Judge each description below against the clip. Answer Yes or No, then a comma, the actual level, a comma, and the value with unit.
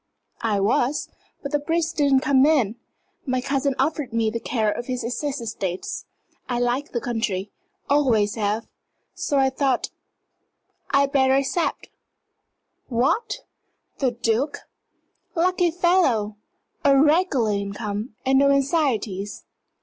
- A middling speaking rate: No, slow, 125 wpm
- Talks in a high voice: Yes, very high, 265 Hz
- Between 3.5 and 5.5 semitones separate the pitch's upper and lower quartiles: Yes, average, 4.3 semitones